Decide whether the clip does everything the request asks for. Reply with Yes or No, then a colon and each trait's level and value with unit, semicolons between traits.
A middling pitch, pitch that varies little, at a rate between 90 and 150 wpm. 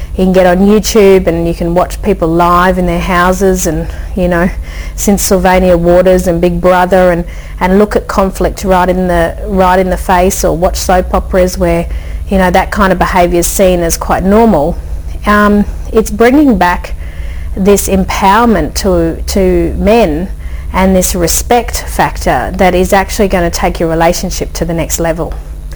No: medium, 180 Hz; narrow, 2.1 semitones; average, 175 wpm